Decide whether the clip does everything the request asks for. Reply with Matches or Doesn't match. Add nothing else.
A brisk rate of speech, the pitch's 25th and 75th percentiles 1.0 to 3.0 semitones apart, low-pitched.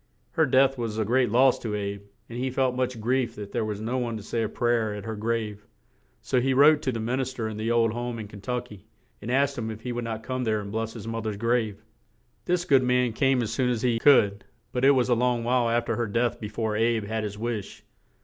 Matches